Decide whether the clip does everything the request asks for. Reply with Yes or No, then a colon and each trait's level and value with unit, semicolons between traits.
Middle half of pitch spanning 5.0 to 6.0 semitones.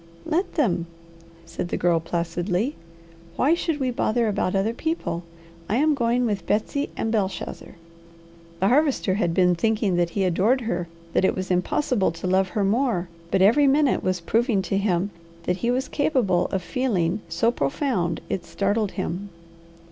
Yes: wide, 5.5 semitones